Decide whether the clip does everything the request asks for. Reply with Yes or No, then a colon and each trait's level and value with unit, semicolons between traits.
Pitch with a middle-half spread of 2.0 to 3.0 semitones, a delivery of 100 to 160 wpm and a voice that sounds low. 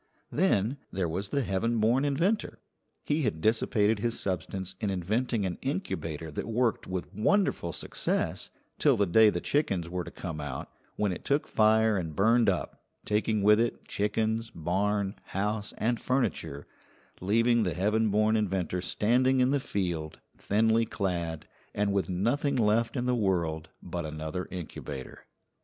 No: average, 4.2 semitones; average, 155 wpm; low, 105 Hz